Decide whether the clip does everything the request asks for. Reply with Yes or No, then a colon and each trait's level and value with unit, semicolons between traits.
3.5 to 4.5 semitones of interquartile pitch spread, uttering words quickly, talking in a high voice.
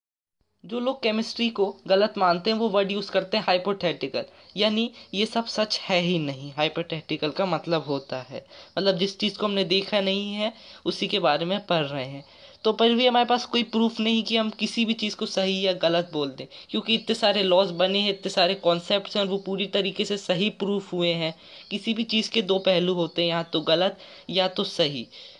Yes: average, 3.9 semitones; fast, 215 wpm; high, 195 Hz